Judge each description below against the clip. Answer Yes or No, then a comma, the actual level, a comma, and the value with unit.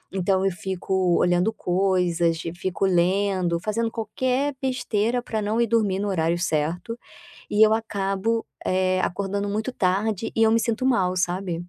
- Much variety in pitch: No, average, 3.6 semitones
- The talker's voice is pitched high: Yes, high, 195 Hz